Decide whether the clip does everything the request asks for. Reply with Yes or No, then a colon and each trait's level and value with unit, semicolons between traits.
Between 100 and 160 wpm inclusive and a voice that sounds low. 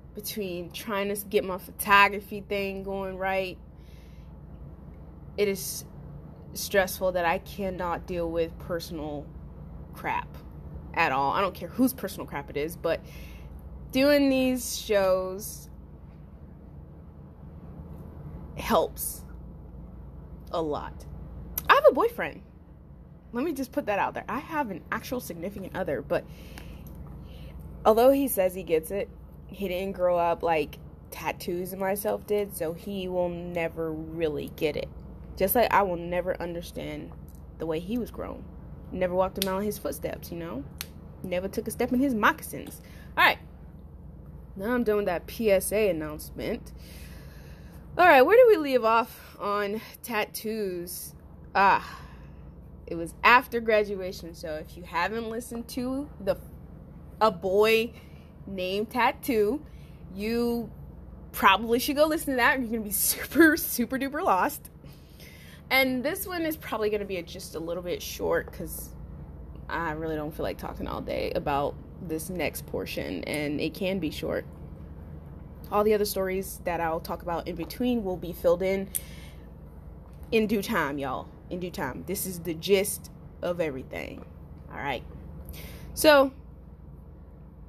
No: average, 145 wpm; medium, 185 Hz